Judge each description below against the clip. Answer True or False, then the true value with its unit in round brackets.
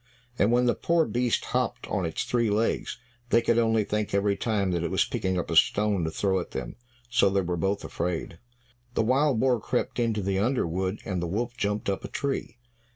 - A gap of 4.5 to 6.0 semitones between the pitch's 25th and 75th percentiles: False (4.0 semitones)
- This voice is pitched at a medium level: False (105 Hz)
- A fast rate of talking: True (220 wpm)